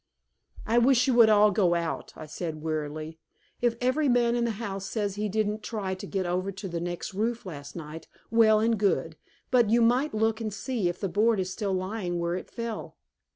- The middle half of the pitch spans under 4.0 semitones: No, average, 4.6 semitones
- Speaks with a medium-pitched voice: No, high, 205 Hz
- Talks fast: Yes, fast, 210 wpm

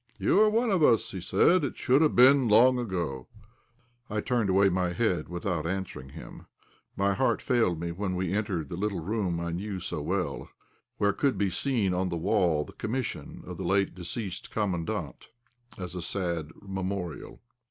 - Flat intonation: No, average, 4.2 semitones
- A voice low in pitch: Yes, very low, 95 Hz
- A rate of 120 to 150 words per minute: No, average, 185 wpm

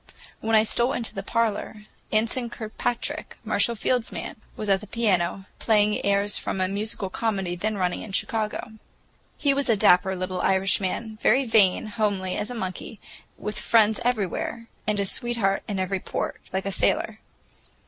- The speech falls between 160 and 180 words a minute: Yes, average, 165 wpm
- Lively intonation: No, average, 2.8 semitones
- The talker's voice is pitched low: No, high, 210 Hz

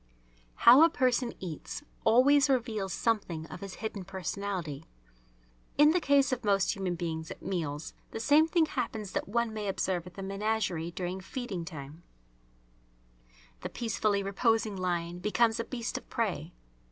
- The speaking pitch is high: Yes, high, 200 Hz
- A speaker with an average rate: Yes, average, 155 wpm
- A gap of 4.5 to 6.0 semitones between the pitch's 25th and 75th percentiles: Yes, average, 4.8 semitones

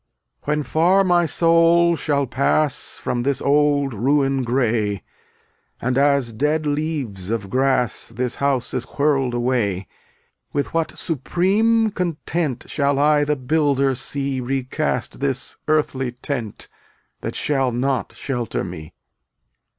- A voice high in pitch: No, medium, 140 Hz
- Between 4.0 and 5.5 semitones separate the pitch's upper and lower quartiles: No, average, 3.5 semitones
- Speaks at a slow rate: Yes, slow, 125 wpm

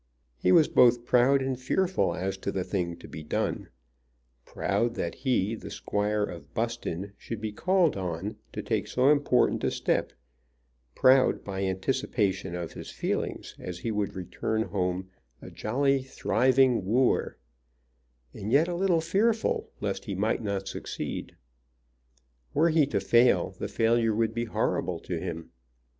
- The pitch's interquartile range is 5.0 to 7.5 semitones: Yes, wide, 5.6 semitones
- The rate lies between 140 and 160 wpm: Yes, average, 150 wpm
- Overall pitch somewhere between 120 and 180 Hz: No, low, 110 Hz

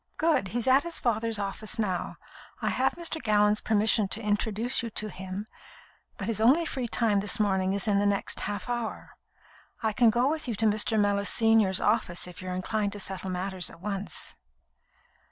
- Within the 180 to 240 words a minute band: Yes, average, 190 wpm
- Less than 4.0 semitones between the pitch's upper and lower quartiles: Yes, narrow, 2.6 semitones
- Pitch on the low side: No, high, 210 Hz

